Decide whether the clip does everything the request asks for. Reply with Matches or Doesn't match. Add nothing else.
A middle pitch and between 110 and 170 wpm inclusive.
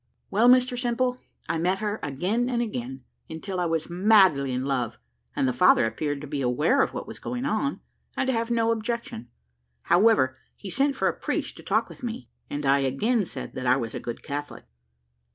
Doesn't match